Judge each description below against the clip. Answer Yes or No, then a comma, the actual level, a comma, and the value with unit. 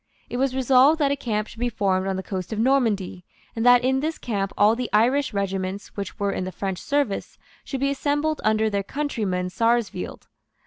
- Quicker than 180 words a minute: Yes, fast, 205 wpm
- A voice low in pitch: No, high, 225 Hz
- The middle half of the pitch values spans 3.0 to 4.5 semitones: No, average, 5.2 semitones